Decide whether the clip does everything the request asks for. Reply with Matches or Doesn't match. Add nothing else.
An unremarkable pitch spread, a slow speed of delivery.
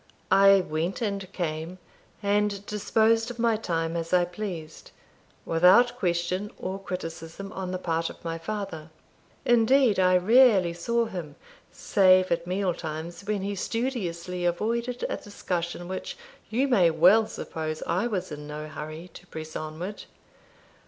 Doesn't match